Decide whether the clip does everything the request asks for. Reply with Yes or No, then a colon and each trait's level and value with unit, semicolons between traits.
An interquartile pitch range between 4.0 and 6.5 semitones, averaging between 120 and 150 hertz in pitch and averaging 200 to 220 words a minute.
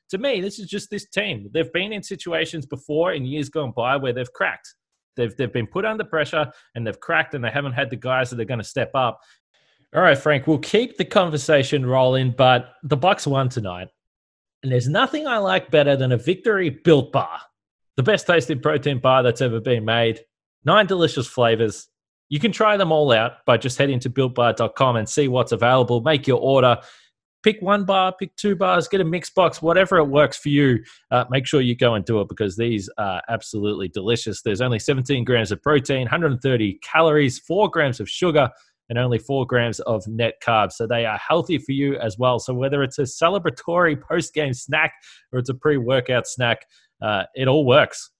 Yes: average, 5.0 semitones; low, 135 Hz; fast, 205 wpm